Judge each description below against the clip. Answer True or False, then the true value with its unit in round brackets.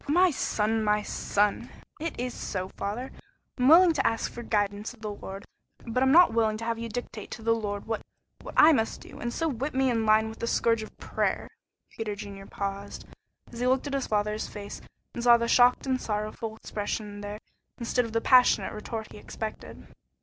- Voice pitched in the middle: False (225 Hz)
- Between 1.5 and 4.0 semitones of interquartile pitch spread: True (2.9 semitones)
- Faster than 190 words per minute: True (200 wpm)